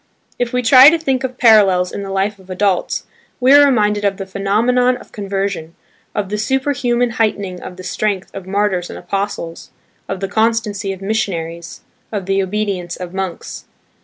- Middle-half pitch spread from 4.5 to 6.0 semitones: No, average, 3.3 semitones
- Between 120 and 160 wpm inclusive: No, average, 175 wpm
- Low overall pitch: No, high, 200 Hz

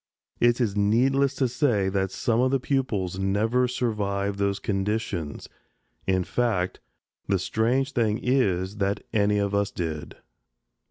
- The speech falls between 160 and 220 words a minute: No, average, 140 wpm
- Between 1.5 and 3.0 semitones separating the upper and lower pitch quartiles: No, average, 4.0 semitones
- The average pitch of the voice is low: Yes, low, 105 Hz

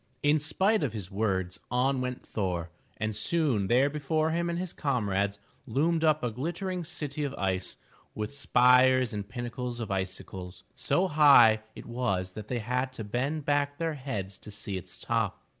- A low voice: Yes, low, 125 Hz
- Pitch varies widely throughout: Yes, wide, 6.2 semitones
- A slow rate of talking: No, average, 175 wpm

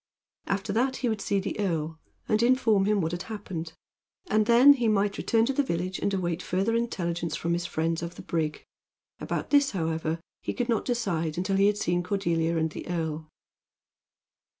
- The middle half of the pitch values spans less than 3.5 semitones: No, average, 4.7 semitones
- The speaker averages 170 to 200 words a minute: Yes, average, 190 wpm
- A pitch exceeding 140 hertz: Yes, high, 190 Hz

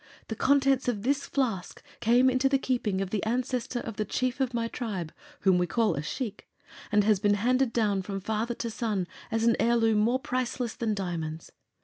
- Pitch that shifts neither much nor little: Yes, average, 3.6 semitones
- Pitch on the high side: Yes, high, 230 Hz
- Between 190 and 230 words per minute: Yes, average, 200 wpm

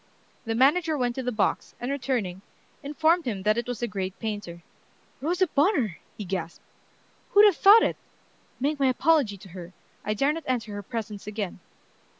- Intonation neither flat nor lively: No, wide, 6.3 semitones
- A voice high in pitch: Yes, high, 240 Hz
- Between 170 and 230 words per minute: Yes, average, 175 wpm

